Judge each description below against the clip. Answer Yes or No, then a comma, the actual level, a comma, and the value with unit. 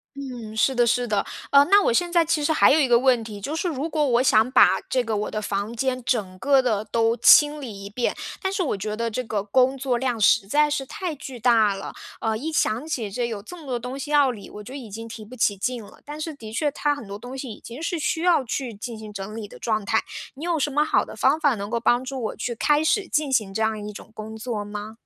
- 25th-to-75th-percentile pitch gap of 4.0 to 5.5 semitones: Yes, average, 4.7 semitones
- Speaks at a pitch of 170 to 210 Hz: No, high, 245 Hz